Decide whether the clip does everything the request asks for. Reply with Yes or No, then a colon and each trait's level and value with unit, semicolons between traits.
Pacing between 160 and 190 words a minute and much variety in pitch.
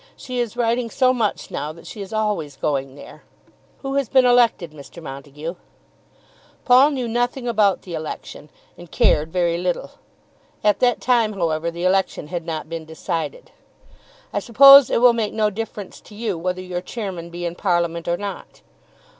Yes: average, 170 wpm; wide, 5.9 semitones